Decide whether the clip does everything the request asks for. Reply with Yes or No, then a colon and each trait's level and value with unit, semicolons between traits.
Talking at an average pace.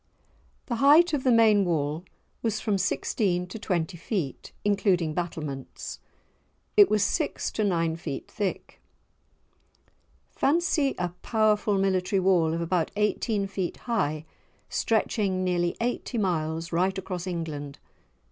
No: slow, 125 wpm